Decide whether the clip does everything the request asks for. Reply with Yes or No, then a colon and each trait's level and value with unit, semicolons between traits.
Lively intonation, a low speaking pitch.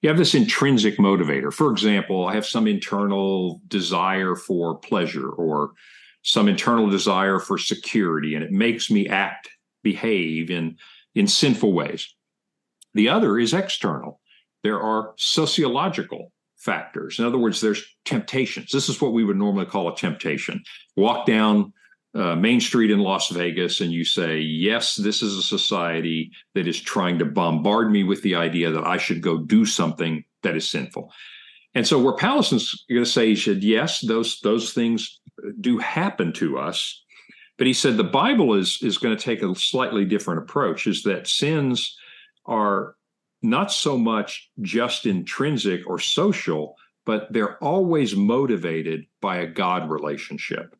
Yes: wide, 6.2 semitones; low, 105 Hz